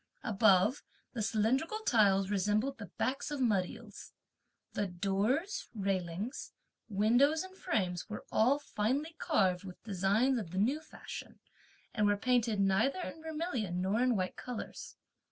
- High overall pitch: Yes, high, 215 Hz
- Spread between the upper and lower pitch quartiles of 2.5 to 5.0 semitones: No, wide, 5.6 semitones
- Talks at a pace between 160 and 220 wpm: No, average, 140 wpm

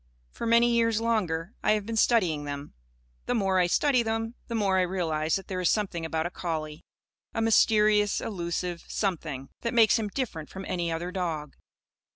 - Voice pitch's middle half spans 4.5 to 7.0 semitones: Yes, average, 5.2 semitones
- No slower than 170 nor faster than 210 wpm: Yes, average, 185 wpm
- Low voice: No, high, 190 Hz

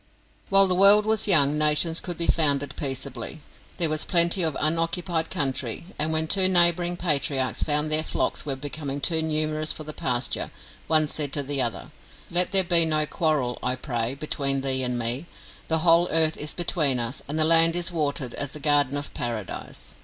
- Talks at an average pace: Yes, average, 190 wpm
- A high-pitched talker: No, medium, 155 Hz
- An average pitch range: Yes, average, 3.4 semitones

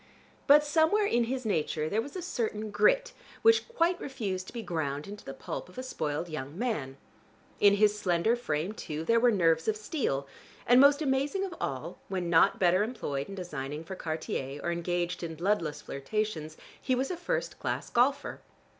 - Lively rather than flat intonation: Yes, wide, 8.0 semitones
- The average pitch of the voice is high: Yes, high, 205 Hz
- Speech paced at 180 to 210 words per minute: Yes, average, 185 wpm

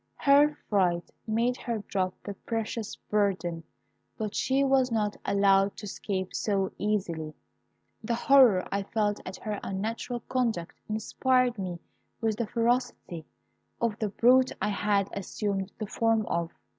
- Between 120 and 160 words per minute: Yes, average, 140 wpm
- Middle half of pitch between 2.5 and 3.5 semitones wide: Yes, average, 3.2 semitones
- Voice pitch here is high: Yes, high, 210 Hz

